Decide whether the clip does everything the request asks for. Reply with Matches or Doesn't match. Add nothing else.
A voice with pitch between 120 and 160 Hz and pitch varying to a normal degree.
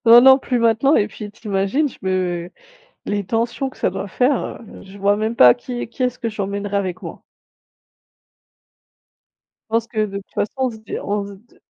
Doesn't match